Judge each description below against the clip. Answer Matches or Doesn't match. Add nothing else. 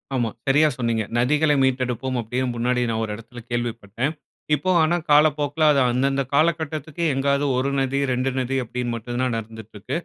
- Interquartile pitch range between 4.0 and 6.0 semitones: Doesn't match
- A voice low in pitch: Matches